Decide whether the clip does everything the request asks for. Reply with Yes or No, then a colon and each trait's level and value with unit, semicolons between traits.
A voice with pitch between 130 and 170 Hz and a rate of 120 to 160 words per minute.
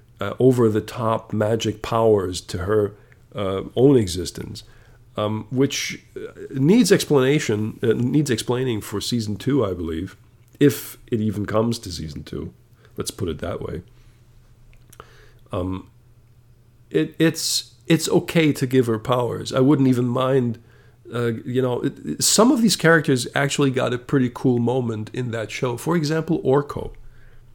No: low, 120 Hz; average, 150 wpm